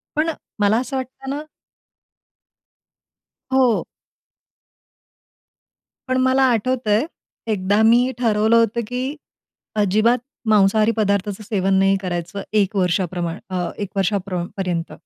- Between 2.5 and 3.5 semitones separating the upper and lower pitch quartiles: No, average, 4.2 semitones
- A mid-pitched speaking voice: No, high, 210 Hz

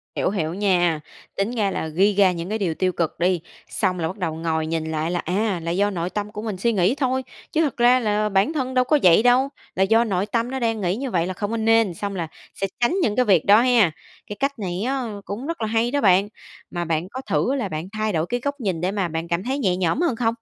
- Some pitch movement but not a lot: Yes, average, 5.0 semitones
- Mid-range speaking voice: No, high, 205 Hz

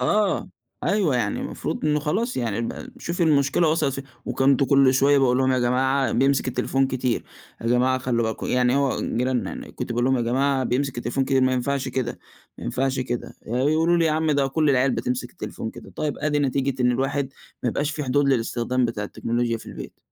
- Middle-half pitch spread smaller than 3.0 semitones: Yes, narrow, 2.4 semitones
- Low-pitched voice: Yes, low, 130 Hz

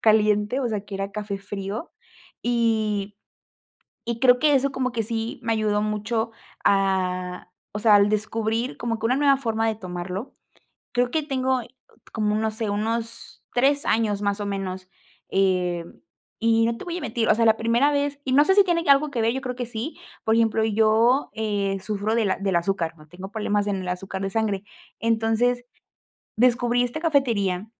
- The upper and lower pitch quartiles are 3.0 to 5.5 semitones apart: Yes, average, 3.3 semitones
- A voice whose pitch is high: Yes, high, 220 Hz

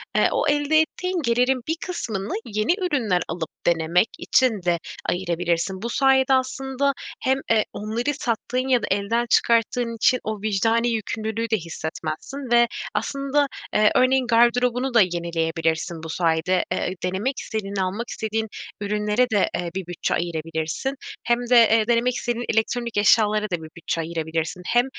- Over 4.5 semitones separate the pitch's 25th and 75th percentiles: Yes, wide, 5.5 semitones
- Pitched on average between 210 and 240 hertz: Yes, high, 220 Hz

